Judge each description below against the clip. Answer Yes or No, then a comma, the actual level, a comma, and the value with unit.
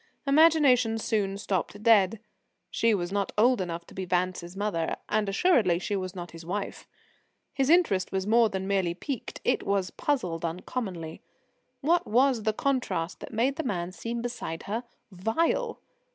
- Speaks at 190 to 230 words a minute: No, average, 160 wpm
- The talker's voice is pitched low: No, high, 205 Hz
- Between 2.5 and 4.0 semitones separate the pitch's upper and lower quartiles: No, average, 5.2 semitones